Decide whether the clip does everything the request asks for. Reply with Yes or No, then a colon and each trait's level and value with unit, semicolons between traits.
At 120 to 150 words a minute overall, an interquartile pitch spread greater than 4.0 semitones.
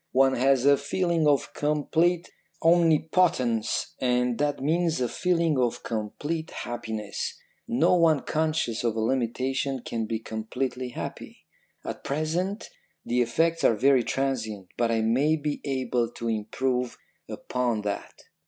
Yes: slow, 135 wpm; average, 4.9 semitones